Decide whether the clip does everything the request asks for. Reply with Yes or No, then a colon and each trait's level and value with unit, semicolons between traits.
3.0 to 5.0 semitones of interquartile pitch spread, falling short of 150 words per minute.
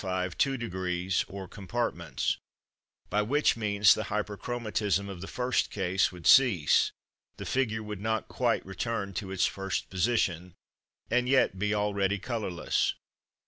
Yes: average, 3.4 semitones; average, 140 wpm